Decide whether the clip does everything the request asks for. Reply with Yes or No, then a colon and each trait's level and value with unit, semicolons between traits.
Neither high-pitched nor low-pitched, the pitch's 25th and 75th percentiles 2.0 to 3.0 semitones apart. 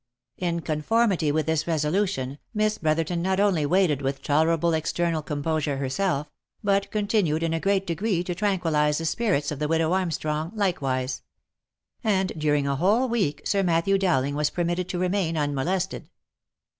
No: medium, 165 Hz; average, 4.1 semitones